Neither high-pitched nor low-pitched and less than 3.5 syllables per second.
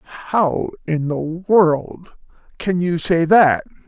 Yes: medium, 170 Hz; 3.3 syllables/s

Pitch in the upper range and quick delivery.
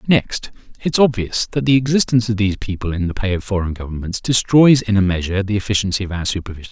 No: low, 105 Hz; fast, 215 wpm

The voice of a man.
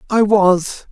Yes: male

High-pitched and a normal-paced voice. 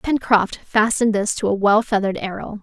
Yes: high, 210 Hz; average, 185 wpm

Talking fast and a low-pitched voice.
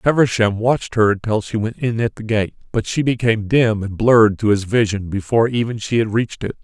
Yes: fast, 225 wpm; low, 110 Hz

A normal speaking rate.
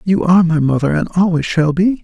No: fast, 235 wpm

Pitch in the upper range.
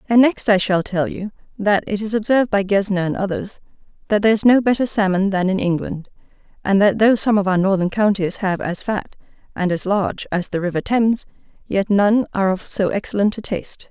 Yes: high, 200 Hz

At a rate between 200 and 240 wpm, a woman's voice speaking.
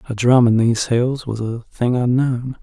No: fast, 205 wpm; male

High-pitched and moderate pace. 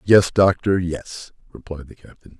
No: very low, 90 Hz; average, 150 wpm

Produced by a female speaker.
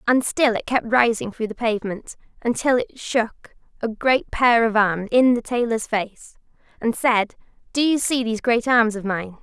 Yes: female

